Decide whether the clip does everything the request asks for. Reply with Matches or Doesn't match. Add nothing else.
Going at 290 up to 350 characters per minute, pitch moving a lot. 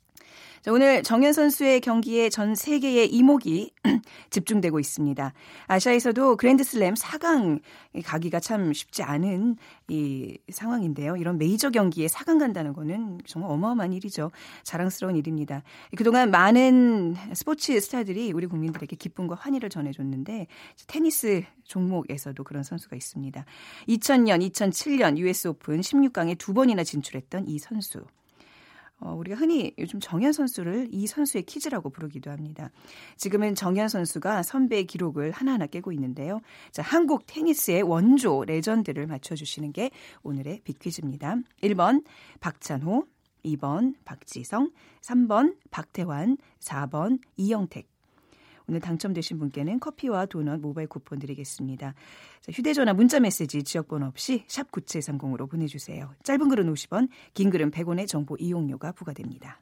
Matches